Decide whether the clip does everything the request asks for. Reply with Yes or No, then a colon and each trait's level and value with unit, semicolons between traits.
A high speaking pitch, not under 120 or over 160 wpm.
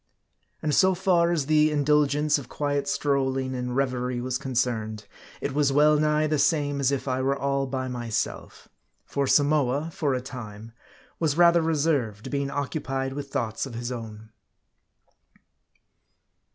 No: medium, 140 Hz; average, 150 wpm